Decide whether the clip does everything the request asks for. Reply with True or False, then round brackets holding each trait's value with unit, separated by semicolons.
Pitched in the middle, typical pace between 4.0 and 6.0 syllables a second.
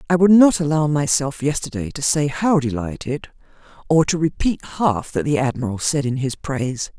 True (145 Hz; 5.0 syllables/s)